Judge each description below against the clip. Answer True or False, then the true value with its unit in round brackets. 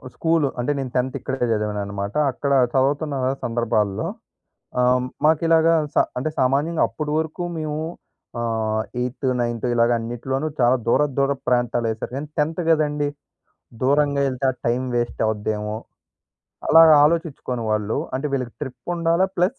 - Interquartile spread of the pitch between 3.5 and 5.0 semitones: True (4.3 semitones)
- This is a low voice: True (130 Hz)